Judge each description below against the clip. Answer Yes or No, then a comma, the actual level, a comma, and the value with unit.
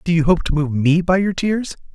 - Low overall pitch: No, medium, 170 Hz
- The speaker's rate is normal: No, fast, 280 wpm